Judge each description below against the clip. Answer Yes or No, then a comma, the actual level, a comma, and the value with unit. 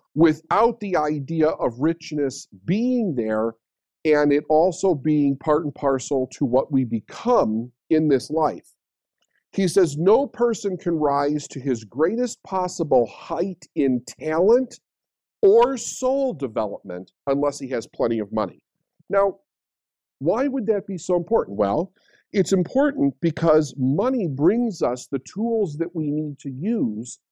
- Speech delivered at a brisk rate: No, average, 140 wpm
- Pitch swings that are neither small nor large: No, wide, 6.3 semitones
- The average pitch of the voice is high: No, medium, 155 Hz